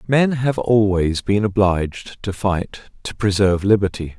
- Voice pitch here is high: No, low, 100 Hz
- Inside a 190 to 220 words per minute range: No, average, 145 wpm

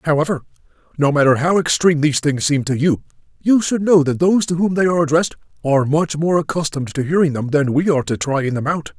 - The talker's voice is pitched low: No, medium, 155 Hz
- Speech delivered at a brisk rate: Yes, fast, 225 wpm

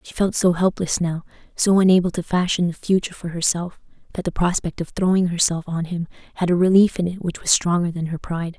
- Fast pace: Yes, fast, 225 wpm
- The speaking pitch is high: No, medium, 175 Hz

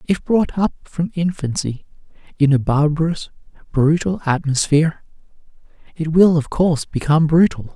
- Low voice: No, medium, 155 Hz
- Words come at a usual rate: No, slow, 125 wpm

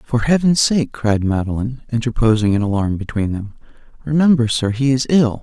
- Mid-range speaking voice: No, low, 120 Hz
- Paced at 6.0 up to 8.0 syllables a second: No, 5.4 syllables/s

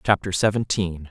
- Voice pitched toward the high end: No, very low, 95 Hz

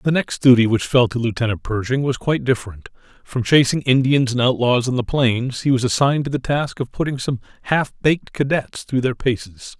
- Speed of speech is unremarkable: No, fast, 210 wpm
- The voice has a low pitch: Yes, low, 125 Hz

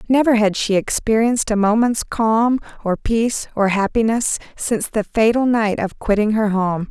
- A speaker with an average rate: Yes, average, 165 wpm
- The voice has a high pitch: Yes, high, 220 Hz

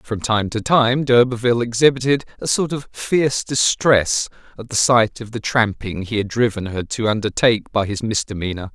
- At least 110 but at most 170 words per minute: No, average, 180 wpm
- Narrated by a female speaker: No, male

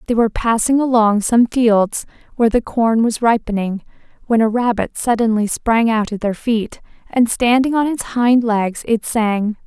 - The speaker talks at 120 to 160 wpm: No, average, 175 wpm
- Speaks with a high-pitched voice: Yes, high, 225 Hz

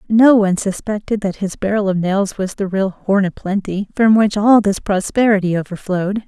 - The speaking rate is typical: Yes, average, 190 wpm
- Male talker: No, female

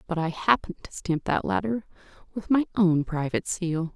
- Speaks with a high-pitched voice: No, medium, 180 Hz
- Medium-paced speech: Yes, average, 180 wpm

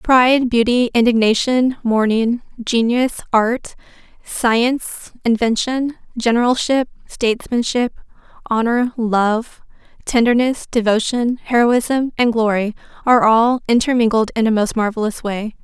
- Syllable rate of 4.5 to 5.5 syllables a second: No, 4.3 syllables/s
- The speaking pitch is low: No, high, 235 Hz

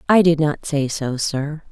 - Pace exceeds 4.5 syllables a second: No, 4.2 syllables/s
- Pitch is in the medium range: Yes, medium, 150 Hz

